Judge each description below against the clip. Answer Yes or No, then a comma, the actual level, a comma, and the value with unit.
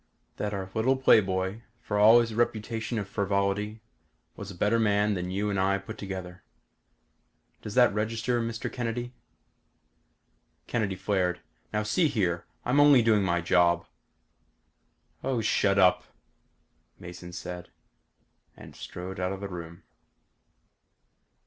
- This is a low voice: Yes, low, 105 Hz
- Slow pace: Yes, slow, 130 wpm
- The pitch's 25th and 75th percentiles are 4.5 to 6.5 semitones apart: No, average, 3.3 semitones